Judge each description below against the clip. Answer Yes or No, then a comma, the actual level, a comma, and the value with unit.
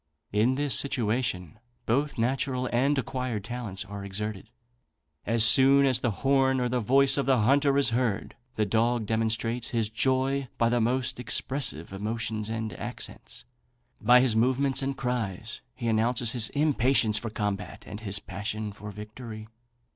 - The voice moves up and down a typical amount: Yes, average, 3.5 semitones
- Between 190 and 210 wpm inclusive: No, average, 150 wpm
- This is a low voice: Yes, low, 115 Hz